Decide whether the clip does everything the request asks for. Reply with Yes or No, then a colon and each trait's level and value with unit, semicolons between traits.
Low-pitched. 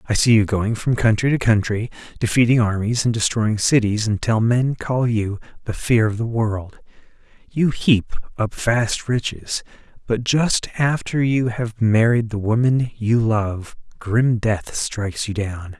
Yes: low, 115 Hz